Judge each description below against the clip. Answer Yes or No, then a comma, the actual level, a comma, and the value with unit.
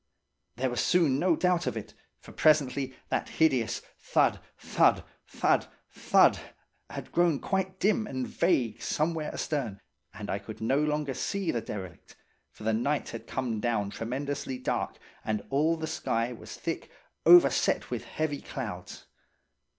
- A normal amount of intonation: No, wide, 5.8 semitones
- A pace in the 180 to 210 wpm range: No, average, 150 wpm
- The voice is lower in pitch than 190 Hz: Yes, low, 135 Hz